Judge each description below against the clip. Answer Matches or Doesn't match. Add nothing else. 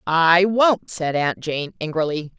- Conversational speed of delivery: Matches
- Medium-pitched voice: Matches